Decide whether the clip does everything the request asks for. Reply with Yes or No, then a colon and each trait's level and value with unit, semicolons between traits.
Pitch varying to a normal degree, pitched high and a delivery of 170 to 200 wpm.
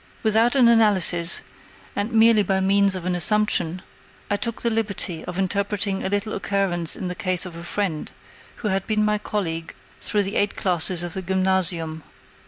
Yes: average, 3.0 semitones; high, 195 Hz; average, 180 wpm